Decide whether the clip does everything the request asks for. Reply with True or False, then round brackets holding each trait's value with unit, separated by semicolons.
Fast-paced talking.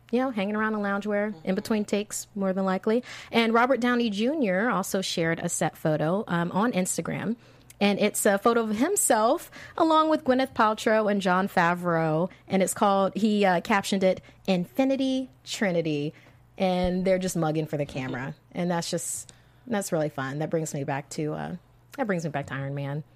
False (185 wpm)